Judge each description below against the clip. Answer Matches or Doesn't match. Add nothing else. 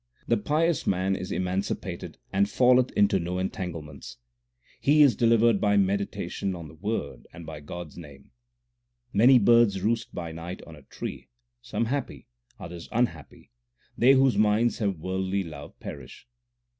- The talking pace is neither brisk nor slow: Matches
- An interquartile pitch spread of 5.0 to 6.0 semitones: Matches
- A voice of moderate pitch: Doesn't match